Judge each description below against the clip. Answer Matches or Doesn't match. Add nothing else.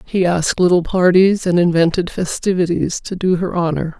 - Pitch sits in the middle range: Matches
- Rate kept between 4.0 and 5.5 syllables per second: Matches